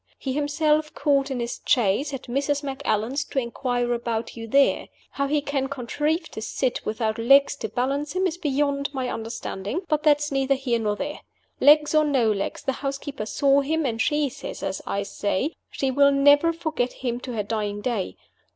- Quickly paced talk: No, average, 190 wpm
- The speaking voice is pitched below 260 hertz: No, very high, 275 Hz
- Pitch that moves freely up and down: No, average, 3.6 semitones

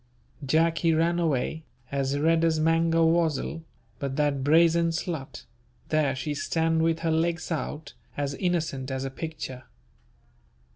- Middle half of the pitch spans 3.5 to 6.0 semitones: No, average, 2.7 semitones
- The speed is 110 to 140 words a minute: Yes, slow, 135 wpm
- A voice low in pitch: No, medium, 160 Hz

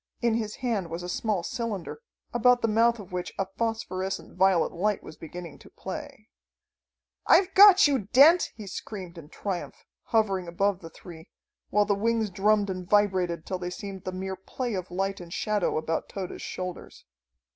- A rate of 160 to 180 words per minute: Yes, average, 175 wpm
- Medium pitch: No, high, 195 Hz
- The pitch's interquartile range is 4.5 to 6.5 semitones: No, average, 3.7 semitones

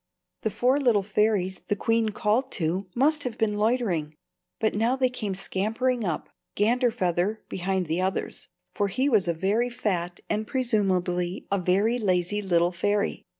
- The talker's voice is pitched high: Yes, high, 205 Hz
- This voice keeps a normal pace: Yes, average, 155 wpm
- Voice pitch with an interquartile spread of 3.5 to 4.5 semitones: Yes, average, 4.0 semitones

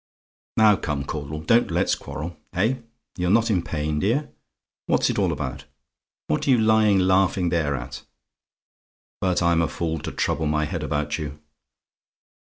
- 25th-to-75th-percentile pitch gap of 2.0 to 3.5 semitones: No, average, 4.6 semitones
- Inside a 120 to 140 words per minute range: No, average, 160 wpm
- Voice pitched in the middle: No, very low, 85 Hz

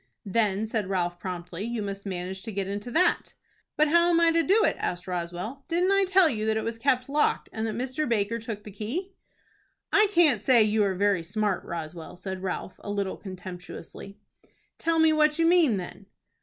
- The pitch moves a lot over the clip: Yes, wide, 8.0 semitones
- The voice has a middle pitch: No, high, 215 Hz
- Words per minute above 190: Yes, average, 200 wpm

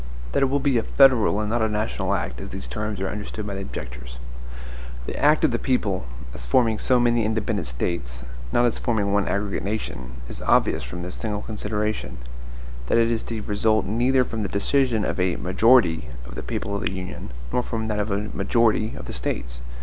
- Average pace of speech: No, fast, 210 wpm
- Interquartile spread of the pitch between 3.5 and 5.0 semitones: Yes, average, 3.8 semitones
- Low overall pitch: Yes, low, 105 Hz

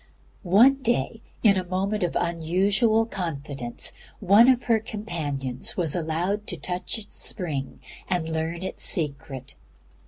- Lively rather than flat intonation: No, average, 4.8 semitones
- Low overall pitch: No, medium, 180 Hz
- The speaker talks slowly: Yes, slow, 130 wpm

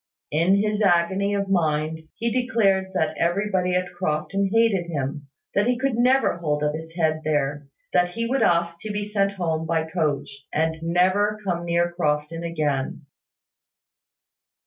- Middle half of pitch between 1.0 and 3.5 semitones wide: No, average, 4.1 semitones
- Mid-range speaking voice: Yes, medium, 175 Hz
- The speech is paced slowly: No, average, 160 wpm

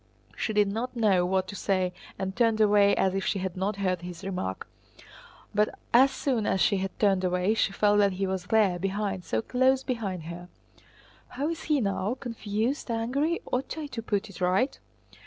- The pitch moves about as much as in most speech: Yes, average, 3.5 semitones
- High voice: Yes, high, 200 Hz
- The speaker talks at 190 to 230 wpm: Yes, average, 195 wpm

